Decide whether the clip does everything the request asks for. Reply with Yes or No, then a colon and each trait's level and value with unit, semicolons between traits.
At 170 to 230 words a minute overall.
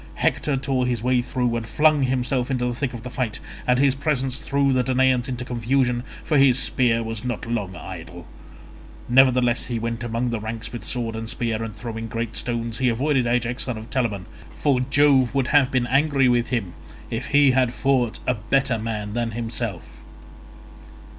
Yes: average, 190 wpm